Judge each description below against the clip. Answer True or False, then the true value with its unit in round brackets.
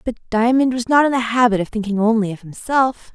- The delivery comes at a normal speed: False (230 wpm)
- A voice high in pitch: True (230 Hz)